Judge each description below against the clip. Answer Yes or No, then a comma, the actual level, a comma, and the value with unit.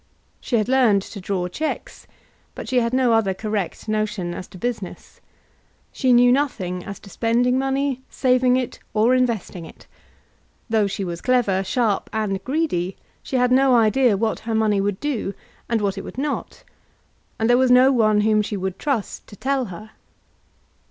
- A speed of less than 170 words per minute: No, average, 175 wpm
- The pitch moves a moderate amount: Yes, average, 4.1 semitones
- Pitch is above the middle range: Yes, high, 225 Hz